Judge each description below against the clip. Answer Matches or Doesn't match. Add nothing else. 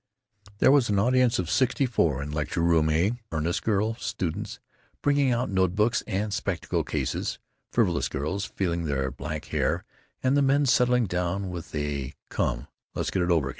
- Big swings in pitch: Matches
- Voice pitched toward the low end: Matches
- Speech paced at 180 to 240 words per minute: Doesn't match